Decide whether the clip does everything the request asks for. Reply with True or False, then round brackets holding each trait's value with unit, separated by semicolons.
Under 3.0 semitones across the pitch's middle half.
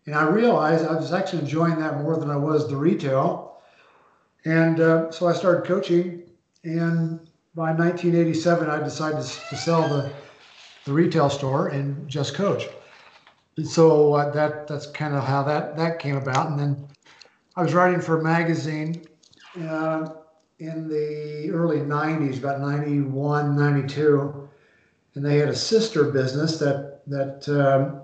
True (2.4 semitones)